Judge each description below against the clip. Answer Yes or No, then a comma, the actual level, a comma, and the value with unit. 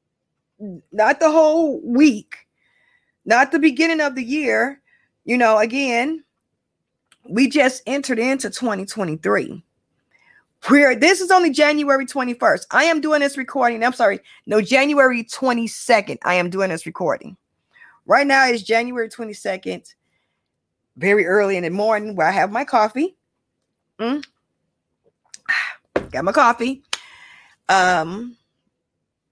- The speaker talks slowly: Yes, slow, 125 wpm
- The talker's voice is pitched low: No, high, 245 Hz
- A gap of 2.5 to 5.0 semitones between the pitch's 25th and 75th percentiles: No, wide, 5.4 semitones